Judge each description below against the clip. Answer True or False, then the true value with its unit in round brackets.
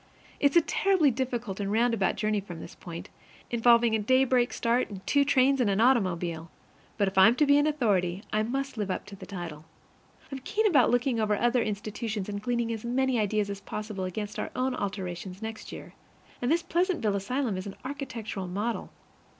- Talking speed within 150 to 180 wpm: False (190 wpm)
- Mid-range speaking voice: False (220 Hz)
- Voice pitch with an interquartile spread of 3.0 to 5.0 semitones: True (4.5 semitones)